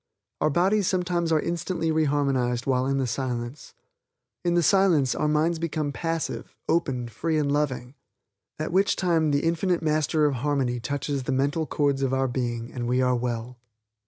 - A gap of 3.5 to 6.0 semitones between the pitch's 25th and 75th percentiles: Yes, average, 4.3 semitones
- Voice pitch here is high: No, medium, 145 Hz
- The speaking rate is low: No, average, 175 wpm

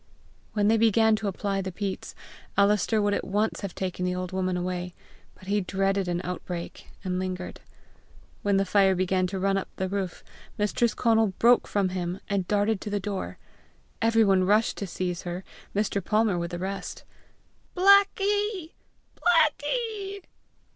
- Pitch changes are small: No, average, 3.2 semitones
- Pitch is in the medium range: No, high, 195 Hz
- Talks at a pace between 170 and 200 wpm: No, average, 160 wpm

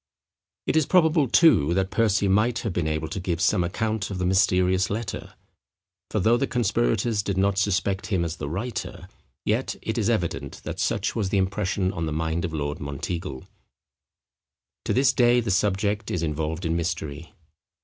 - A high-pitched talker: No, very low, 95 Hz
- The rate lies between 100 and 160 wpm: No, average, 180 wpm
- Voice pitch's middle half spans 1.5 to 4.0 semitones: No, average, 4.6 semitones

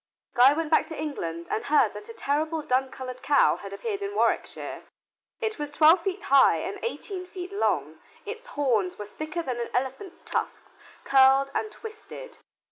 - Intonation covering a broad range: Yes, wide, 6.8 semitones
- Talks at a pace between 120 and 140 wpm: No, average, 175 wpm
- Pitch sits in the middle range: No, very high, 300 Hz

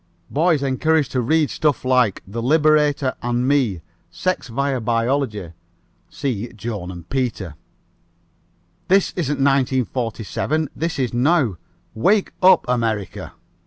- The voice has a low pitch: Yes, low, 130 Hz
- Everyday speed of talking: No, slow, 115 wpm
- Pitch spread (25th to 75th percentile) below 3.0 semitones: No, average, 4.5 semitones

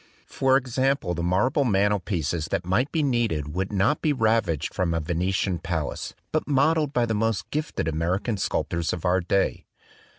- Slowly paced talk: No, average, 165 wpm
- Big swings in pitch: Yes, wide, 6.9 semitones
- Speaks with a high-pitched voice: No, low, 100 Hz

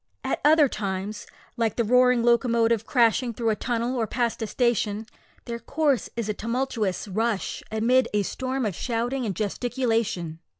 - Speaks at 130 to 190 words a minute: Yes, average, 160 wpm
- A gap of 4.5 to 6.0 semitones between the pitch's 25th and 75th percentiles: No, average, 2.7 semitones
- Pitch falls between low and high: No, high, 230 Hz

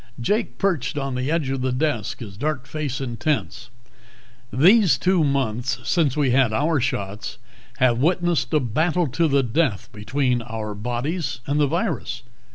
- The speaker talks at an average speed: Yes, average, 160 wpm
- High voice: No, low, 135 Hz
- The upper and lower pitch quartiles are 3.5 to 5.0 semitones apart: Yes, average, 4.4 semitones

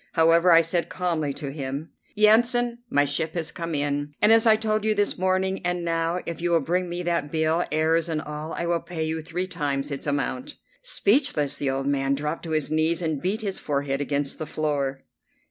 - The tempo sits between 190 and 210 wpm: Yes, fast, 205 wpm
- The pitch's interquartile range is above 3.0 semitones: Yes, average, 3.7 semitones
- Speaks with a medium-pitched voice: Yes, medium, 165 Hz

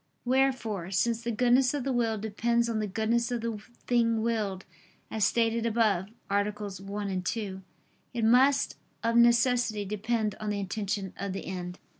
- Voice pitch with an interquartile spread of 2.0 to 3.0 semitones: Yes, average, 2.7 semitones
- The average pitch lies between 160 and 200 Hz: No, high, 220 Hz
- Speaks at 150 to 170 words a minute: Yes, average, 160 wpm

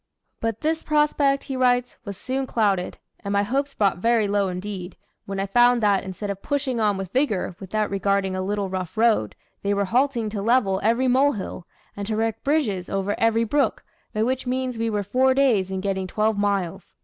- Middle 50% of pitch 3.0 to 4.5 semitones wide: Yes, average, 4.2 semitones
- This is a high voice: Yes, high, 215 Hz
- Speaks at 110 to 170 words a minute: No, average, 195 wpm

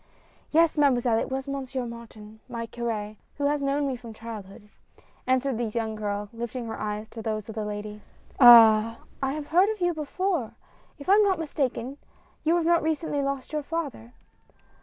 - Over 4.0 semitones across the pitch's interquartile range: Yes, average, 4.9 semitones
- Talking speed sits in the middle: Yes, average, 180 wpm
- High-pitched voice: Yes, very high, 250 Hz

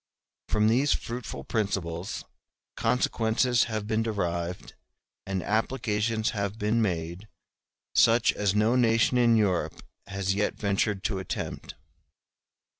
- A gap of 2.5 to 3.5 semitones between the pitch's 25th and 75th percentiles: Yes, average, 2.8 semitones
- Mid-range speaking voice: No, low, 105 Hz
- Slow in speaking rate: Yes, slow, 115 wpm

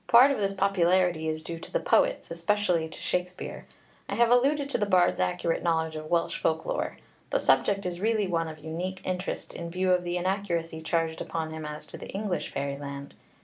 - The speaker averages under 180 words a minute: No, average, 200 wpm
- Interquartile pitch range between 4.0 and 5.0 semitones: No, average, 3.5 semitones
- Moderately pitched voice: Yes, medium, 175 Hz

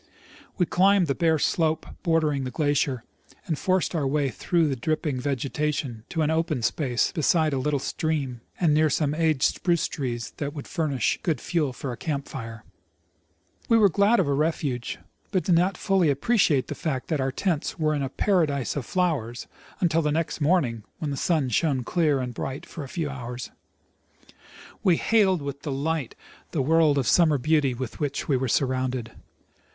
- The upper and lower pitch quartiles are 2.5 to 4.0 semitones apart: Yes, average, 3.7 semitones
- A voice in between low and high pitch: Yes, medium, 150 Hz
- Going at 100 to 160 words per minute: No, average, 185 wpm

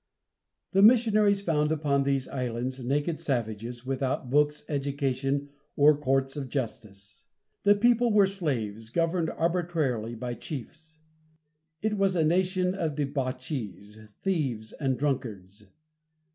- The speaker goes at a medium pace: No, slow, 115 wpm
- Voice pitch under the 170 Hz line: Yes, medium, 140 Hz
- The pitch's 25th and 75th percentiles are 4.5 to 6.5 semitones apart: Yes, average, 5.2 semitones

